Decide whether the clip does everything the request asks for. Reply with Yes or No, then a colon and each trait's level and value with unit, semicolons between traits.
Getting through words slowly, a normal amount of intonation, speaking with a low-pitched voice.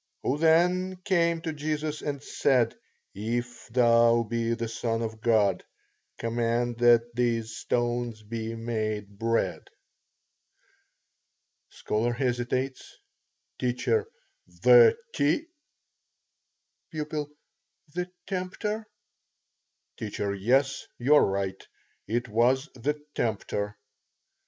Yes: slow, 95 wpm; average, 4.5 semitones; low, 120 Hz